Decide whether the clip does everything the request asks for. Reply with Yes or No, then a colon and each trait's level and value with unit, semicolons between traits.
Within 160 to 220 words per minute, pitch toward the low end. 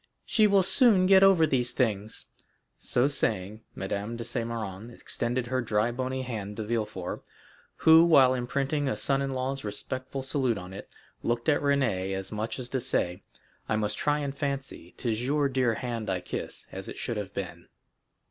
Yes: average, 180 wpm; low, 125 Hz